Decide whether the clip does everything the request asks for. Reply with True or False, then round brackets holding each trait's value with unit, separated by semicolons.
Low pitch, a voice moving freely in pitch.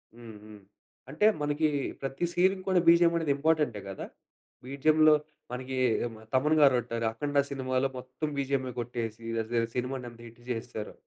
False (130 Hz; 4.1 semitones)